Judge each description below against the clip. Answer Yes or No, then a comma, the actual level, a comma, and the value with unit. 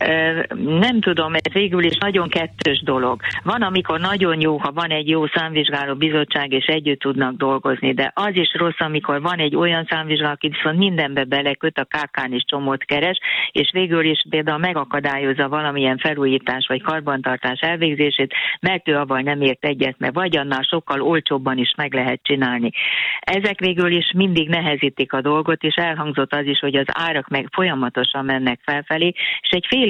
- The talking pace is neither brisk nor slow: No, fast, 170 wpm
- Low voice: No, medium, 150 Hz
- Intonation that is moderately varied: Yes, average, 3.4 semitones